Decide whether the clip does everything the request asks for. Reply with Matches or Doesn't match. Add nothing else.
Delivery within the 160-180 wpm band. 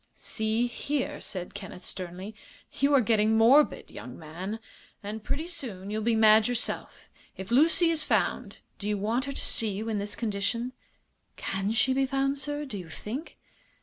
Matches